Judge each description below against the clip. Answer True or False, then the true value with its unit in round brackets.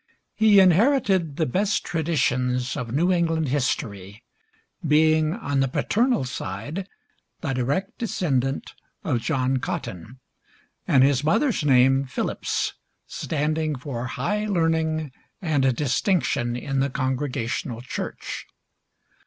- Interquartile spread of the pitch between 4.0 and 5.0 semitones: True (4.6 semitones)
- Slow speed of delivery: True (110 wpm)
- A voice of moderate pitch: True (145 Hz)